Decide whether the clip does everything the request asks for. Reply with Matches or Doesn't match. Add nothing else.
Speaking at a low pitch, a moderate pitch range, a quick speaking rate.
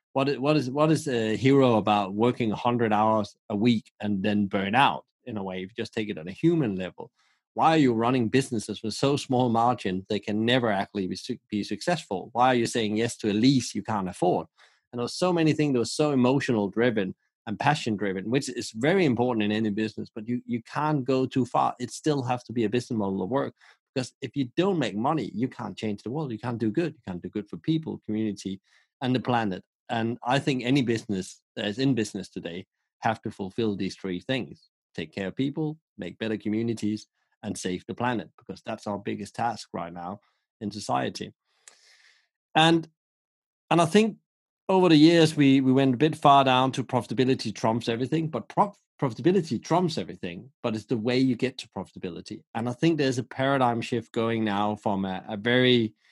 Matches